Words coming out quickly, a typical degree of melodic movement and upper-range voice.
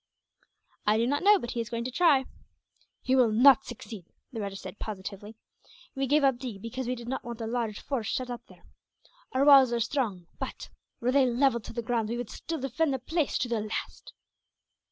Yes: fast, 215 wpm; average, 3.0 semitones; high, 240 Hz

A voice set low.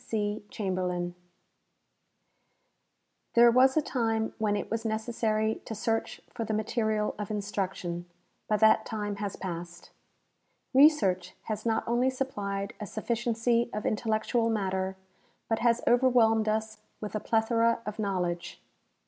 No: high, 220 Hz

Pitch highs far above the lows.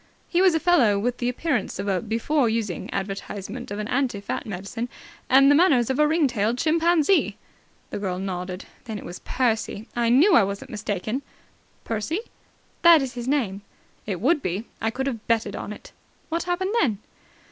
Yes: wide, 6.1 semitones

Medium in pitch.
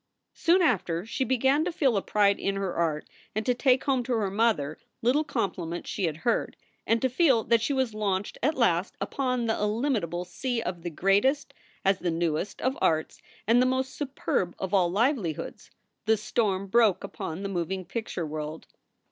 No: high, 215 Hz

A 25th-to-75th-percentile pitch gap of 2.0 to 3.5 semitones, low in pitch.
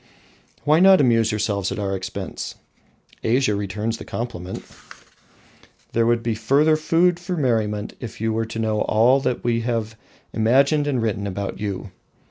No: average, 3.9 semitones; low, 115 Hz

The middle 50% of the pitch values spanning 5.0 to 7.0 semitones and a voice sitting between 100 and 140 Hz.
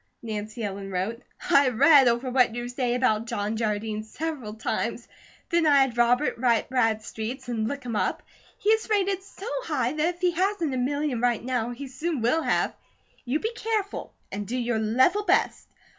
No: average, 5.3 semitones; very high, 250 Hz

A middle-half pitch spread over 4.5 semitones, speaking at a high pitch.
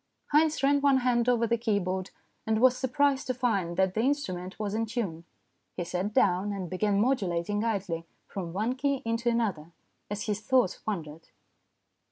Yes: average, 5.0 semitones; high, 215 Hz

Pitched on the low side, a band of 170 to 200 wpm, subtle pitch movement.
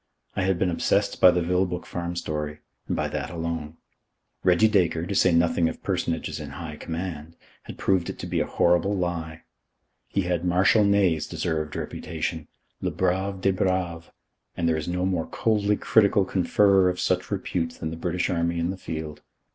Yes: very low, 90 Hz; average, 180 wpm; narrow, 2.3 semitones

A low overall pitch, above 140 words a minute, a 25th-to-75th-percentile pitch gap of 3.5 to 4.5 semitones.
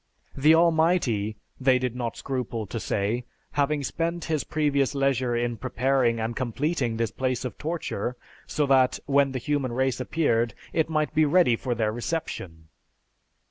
Yes: low, 130 Hz; average, 155 wpm; average, 4.1 semitones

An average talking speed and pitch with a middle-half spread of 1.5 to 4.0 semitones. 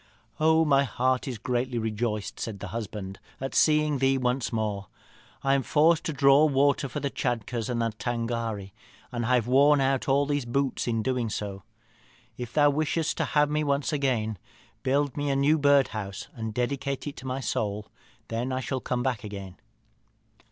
Yes: average, 180 wpm; average, 3.6 semitones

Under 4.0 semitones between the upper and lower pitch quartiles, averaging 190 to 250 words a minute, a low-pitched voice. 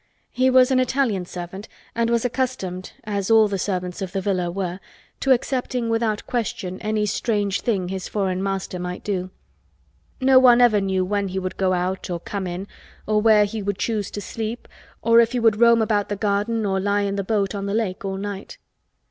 No: average, 3.2 semitones; fast, 205 wpm; high, 205 Hz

